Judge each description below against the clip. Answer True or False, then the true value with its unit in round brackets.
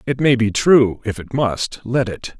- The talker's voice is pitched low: True (120 Hz)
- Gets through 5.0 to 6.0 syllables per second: False (4.1 syllables/s)